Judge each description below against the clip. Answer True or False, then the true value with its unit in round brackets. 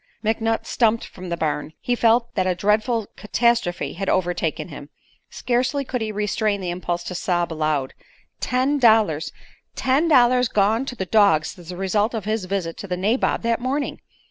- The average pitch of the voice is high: True (210 Hz)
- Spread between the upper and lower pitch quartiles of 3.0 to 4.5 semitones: False (5.0 semitones)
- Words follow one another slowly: False (175 wpm)